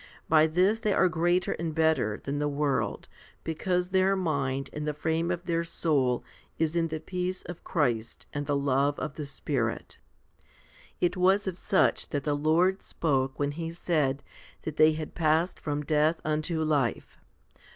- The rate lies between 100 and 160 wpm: No, average, 170 wpm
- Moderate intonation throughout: Yes, average, 3.2 semitones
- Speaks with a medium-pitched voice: Yes, medium, 155 Hz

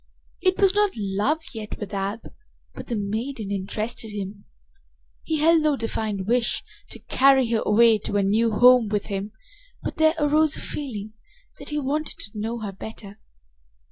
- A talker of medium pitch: No, high, 225 Hz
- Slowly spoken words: No, average, 170 wpm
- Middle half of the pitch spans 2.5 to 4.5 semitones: No, average, 5.3 semitones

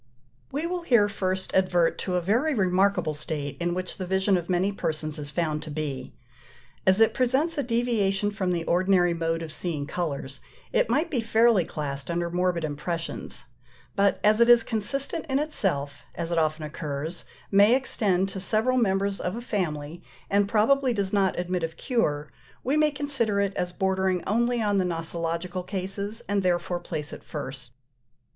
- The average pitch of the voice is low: No, medium, 185 Hz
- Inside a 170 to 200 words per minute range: Yes, average, 175 wpm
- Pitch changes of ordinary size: Yes, average, 4.8 semitones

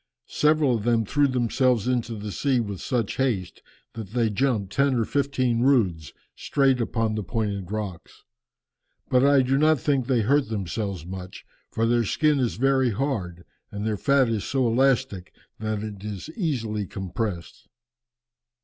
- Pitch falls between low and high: No, low, 115 Hz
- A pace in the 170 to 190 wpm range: No, average, 160 wpm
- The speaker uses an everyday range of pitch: Yes, average, 4.5 semitones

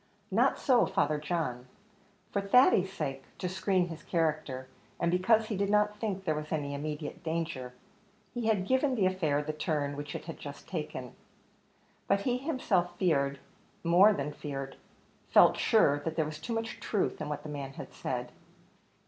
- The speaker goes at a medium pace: Yes, average, 175 wpm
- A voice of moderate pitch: Yes, medium, 165 Hz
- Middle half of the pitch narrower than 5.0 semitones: No, average, 5.3 semitones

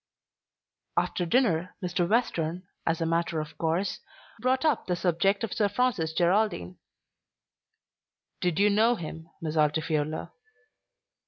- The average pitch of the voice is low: No, medium, 175 Hz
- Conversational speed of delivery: No, slow, 120 wpm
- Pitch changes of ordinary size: Yes, average, 4.4 semitones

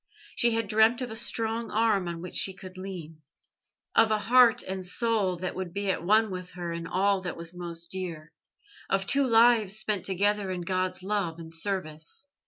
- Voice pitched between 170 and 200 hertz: Yes, high, 190 Hz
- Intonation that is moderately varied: Yes, average, 3.7 semitones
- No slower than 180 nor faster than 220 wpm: Yes, average, 190 wpm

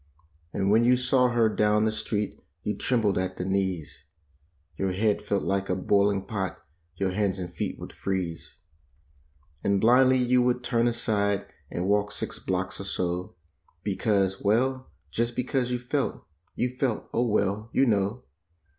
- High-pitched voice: No, low, 105 Hz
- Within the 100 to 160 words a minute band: Yes, average, 155 wpm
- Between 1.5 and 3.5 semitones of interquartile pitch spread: No, average, 3.9 semitones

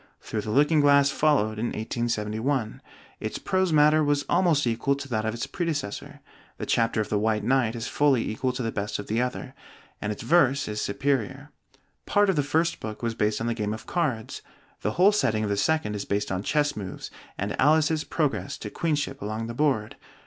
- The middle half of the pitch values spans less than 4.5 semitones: No, average, 5.3 semitones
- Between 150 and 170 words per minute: No, fast, 205 wpm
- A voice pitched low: Yes, low, 125 Hz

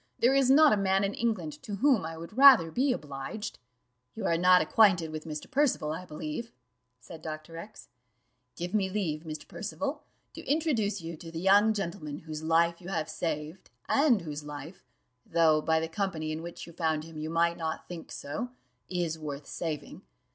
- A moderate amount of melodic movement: Yes, average, 4.8 semitones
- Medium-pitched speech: Yes, medium, 170 Hz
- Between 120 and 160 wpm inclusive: No, average, 185 wpm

